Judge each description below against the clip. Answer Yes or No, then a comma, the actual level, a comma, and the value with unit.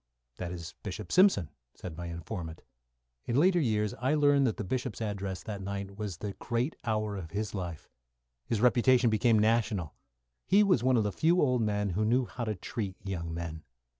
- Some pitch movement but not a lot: Yes, average, 4.7 semitones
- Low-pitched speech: Yes, low, 105 Hz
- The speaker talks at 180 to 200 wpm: Yes, average, 190 wpm